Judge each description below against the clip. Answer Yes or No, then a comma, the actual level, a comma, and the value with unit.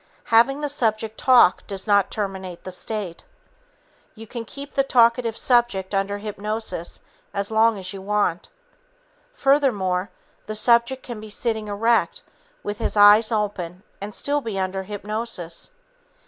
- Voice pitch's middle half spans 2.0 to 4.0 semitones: Yes, average, 3.1 semitones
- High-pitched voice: Yes, high, 215 Hz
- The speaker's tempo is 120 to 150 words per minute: Yes, average, 140 wpm